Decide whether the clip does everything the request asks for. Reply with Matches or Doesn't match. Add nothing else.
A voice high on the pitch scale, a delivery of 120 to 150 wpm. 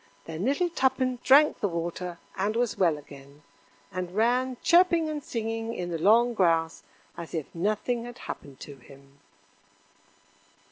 Matches